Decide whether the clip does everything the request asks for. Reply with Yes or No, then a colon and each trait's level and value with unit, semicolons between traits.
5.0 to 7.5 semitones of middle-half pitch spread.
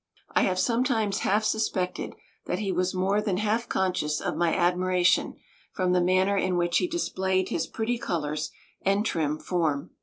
No: average, 2.9 semitones